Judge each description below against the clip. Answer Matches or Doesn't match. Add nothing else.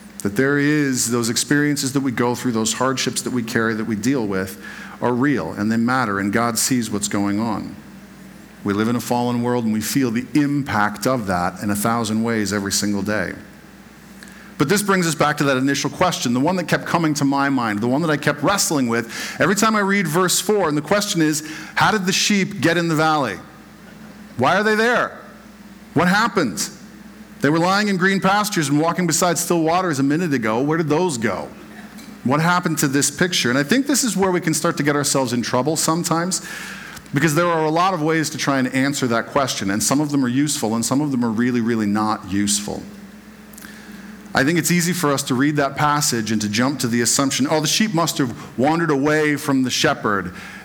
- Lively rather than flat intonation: Matches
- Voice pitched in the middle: Matches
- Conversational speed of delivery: Doesn't match